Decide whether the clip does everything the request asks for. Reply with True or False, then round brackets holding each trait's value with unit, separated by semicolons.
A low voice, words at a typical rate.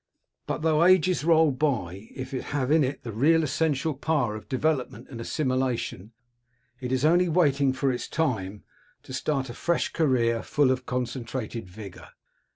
True (130 Hz; 165 wpm)